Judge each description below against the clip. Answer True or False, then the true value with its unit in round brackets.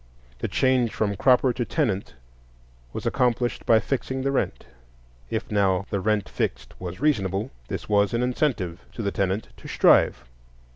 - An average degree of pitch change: True (4.4 semitones)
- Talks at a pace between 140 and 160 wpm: True (155 wpm)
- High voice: False (110 Hz)